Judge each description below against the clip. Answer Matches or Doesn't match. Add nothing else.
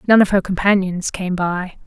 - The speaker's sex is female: Matches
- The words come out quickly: Doesn't match